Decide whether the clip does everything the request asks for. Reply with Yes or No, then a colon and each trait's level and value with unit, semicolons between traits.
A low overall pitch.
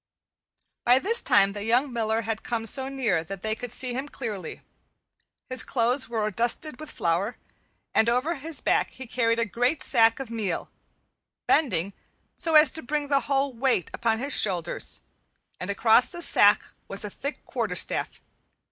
No: high, 235 Hz